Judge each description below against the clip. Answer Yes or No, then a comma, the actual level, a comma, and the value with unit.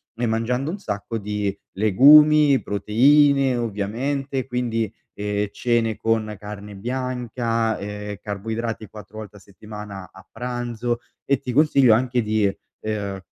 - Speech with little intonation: No, average, 3.2 semitones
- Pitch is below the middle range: Yes, low, 115 Hz